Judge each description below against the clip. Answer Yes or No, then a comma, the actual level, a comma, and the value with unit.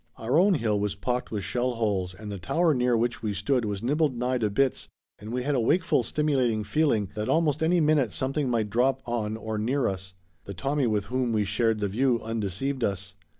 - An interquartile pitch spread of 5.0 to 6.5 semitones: No, average, 4.3 semitones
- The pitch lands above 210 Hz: No, low, 120 Hz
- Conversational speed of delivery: No, fast, 215 wpm